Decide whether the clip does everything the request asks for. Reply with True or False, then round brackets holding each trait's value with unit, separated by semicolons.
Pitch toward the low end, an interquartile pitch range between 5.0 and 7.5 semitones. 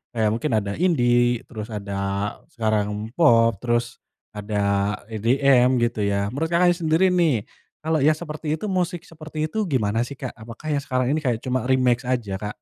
True (125 Hz; 5.5 semitones)